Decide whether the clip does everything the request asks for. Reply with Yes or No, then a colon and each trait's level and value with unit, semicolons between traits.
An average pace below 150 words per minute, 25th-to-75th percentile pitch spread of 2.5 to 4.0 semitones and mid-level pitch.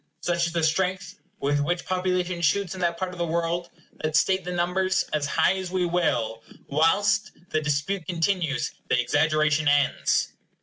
No: average, 170 wpm; average, 3.1 semitones; medium, 170 Hz